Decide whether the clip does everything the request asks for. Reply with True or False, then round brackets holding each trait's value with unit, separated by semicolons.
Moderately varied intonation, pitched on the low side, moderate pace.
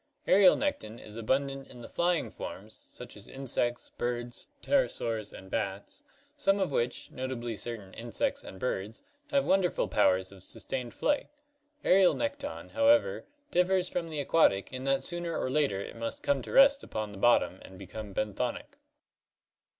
False (8.6 semitones; 125 Hz; 160 wpm)